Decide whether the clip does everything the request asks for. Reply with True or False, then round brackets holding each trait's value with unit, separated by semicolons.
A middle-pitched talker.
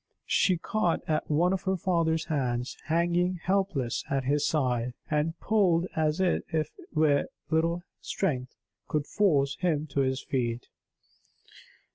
True (155 Hz)